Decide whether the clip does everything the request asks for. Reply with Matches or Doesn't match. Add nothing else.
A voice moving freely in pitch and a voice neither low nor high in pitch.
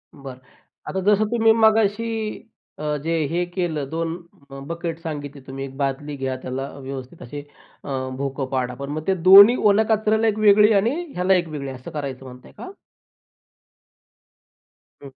Matches